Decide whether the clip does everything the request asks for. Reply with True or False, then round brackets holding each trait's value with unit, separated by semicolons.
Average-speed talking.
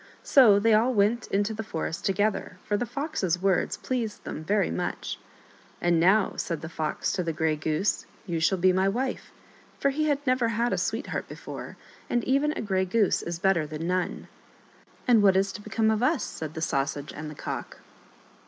False (210 wpm)